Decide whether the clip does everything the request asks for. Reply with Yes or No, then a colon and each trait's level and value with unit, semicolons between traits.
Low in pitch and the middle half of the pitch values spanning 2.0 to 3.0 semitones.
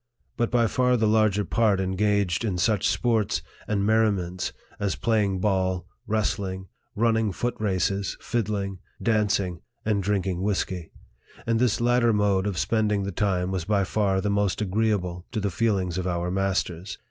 Yes: low, 100 Hz; average, 2.7 semitones